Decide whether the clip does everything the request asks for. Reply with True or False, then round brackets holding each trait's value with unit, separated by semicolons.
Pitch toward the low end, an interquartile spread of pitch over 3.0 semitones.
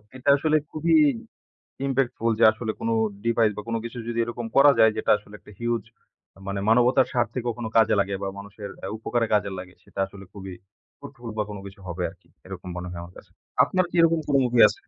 True (115 Hz; 3.4 semitones)